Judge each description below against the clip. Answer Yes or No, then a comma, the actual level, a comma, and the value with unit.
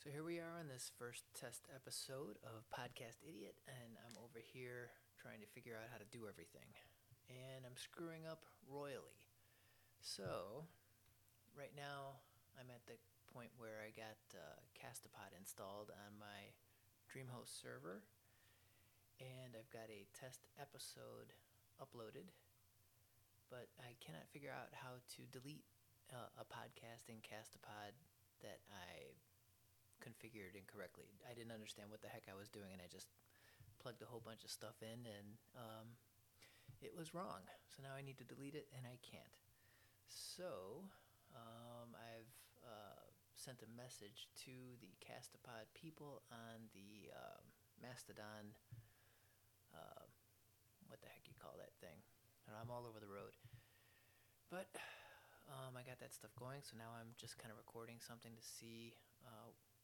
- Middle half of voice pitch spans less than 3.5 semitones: Yes, narrow, 2.5 semitones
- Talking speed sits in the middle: Yes, average, 150 wpm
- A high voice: No, low, 115 Hz